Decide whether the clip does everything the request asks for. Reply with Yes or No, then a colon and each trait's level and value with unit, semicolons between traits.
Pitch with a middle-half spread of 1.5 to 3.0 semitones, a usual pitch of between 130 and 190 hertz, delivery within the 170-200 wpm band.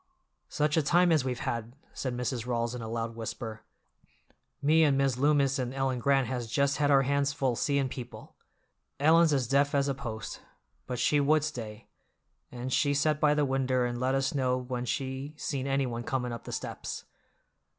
Yes: narrow, 2.5 semitones; low, 135 Hz; average, 190 wpm